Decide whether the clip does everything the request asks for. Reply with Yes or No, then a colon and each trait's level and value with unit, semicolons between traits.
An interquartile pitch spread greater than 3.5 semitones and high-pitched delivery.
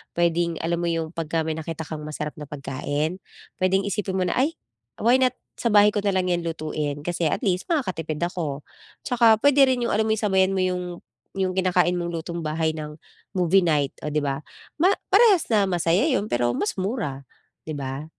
No: average, 4.2 semitones; medium, 175 Hz